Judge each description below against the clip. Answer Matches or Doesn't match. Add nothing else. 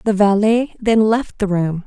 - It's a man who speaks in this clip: Doesn't match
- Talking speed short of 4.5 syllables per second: Matches